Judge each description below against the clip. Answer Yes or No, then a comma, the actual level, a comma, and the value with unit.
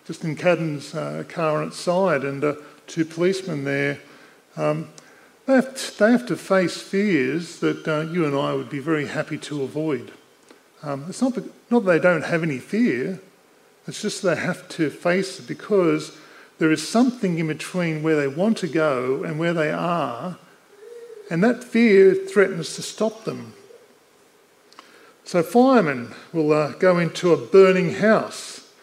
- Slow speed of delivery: No, average, 170 wpm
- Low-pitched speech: No, medium, 175 Hz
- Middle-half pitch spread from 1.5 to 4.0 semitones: No, average, 5.0 semitones